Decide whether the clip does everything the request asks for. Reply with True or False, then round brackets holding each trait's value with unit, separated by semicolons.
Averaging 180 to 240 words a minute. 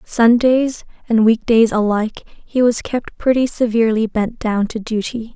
False (155 wpm)